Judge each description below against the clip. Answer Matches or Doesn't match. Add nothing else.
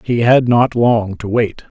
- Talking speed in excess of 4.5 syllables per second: Doesn't match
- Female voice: Doesn't match